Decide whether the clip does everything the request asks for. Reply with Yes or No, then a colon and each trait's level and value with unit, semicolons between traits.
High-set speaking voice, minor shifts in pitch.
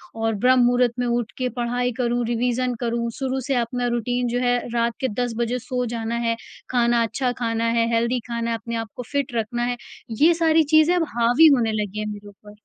Yes: high, 240 Hz; narrow, 1.4 semitones